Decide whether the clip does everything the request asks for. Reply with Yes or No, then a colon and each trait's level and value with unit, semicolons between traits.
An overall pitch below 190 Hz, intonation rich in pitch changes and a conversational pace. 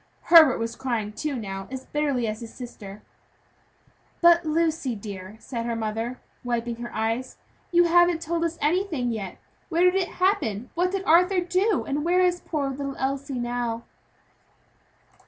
No: very high, 270 Hz; wide, 6.8 semitones; average, 155 wpm